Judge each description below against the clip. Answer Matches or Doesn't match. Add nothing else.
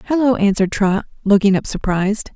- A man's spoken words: Doesn't match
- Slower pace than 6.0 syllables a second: Doesn't match